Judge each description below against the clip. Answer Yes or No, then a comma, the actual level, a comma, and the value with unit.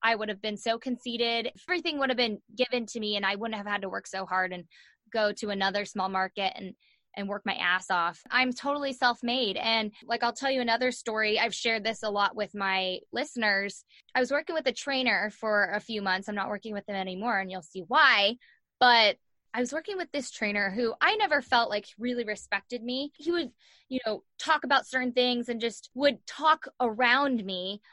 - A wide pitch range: No, average, 3.7 semitones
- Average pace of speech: No, fast, 215 wpm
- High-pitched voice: Yes, high, 225 Hz